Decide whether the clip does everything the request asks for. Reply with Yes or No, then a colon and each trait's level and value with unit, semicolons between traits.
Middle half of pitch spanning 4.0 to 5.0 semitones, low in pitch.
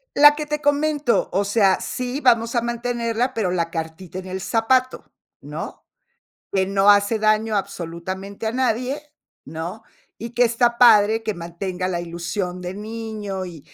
No: average, 4.3 semitones; high, 215 Hz